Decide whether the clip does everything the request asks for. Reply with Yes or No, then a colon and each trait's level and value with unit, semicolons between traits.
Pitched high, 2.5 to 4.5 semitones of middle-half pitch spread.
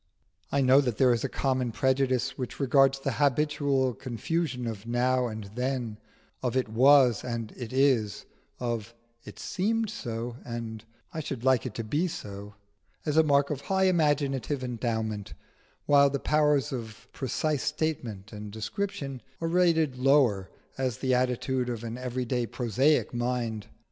No: low, 130 Hz; average, 3.3 semitones